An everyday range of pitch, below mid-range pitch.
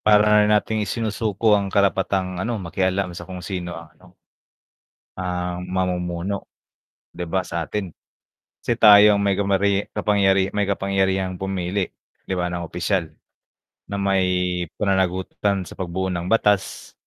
No: narrow, 2.0 semitones; very low, 95 Hz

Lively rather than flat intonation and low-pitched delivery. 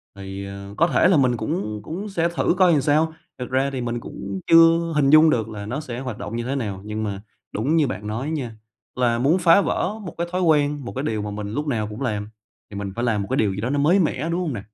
Yes: wide, 6.9 semitones; low, 130 Hz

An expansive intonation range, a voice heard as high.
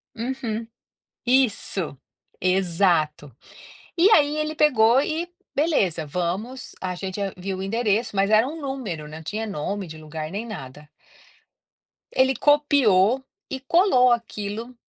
Yes: wide, 6.4 semitones; high, 215 Hz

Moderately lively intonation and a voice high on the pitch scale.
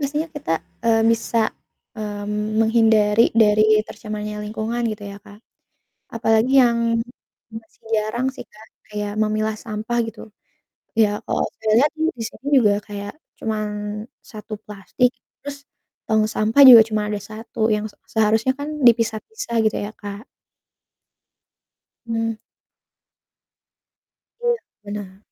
No: narrow, 1.6 semitones; high, 220 Hz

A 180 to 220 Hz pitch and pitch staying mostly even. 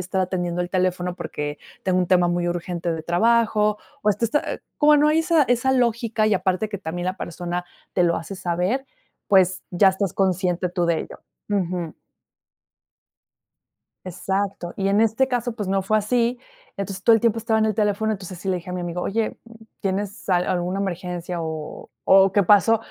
No: high, 190 Hz; average, 3.4 semitones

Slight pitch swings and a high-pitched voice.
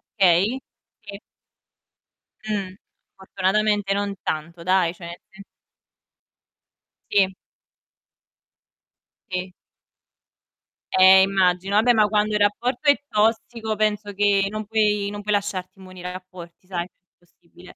Yes: narrow, 2.3 semitones; high, 200 Hz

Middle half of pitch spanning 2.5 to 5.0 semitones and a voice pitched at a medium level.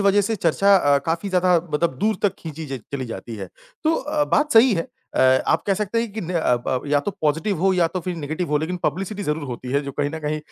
No: wide, 5.6 semitones; medium, 170 Hz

